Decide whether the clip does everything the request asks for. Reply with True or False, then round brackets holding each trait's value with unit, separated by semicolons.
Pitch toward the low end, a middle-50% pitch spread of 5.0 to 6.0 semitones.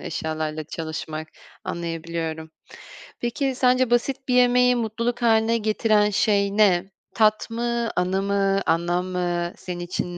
False (200 Hz; 5.3 semitones)